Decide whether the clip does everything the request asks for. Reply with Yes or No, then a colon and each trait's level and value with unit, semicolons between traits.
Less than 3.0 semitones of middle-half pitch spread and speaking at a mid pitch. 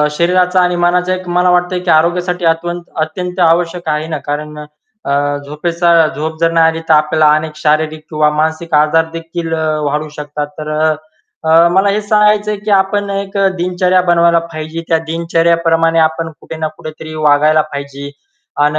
Yes: narrow, 2.4 semitones; medium, 165 Hz